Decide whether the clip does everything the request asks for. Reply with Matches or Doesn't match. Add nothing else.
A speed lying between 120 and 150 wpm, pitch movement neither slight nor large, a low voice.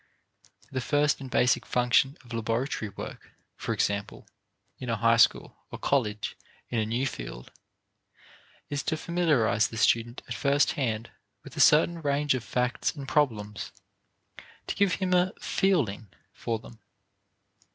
Matches